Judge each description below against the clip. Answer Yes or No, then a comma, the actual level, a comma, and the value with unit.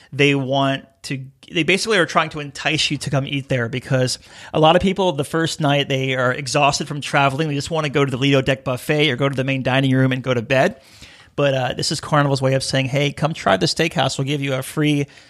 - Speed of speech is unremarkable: No, fast, 260 wpm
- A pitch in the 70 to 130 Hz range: No, medium, 140 Hz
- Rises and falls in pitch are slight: Yes, narrow, 2.2 semitones